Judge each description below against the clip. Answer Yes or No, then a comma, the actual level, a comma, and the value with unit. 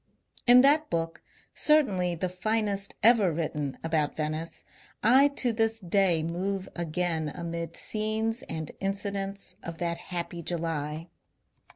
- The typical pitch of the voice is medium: Yes, medium, 180 Hz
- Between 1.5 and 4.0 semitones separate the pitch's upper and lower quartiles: No, average, 4.6 semitones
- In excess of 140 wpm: No, slow, 135 wpm